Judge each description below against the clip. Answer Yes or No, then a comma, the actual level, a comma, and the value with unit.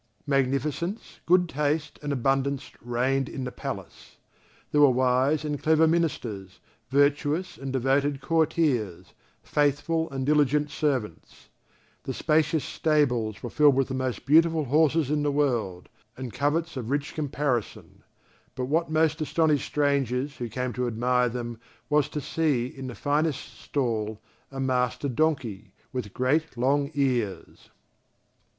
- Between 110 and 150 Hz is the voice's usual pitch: Yes, medium, 140 Hz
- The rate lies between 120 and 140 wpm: Yes, slow, 135 wpm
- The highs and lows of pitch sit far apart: No, average, 3.1 semitones